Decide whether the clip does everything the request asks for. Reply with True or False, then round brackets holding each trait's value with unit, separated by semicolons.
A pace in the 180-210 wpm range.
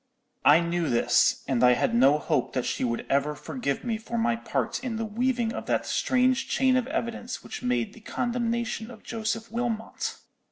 True (190 wpm)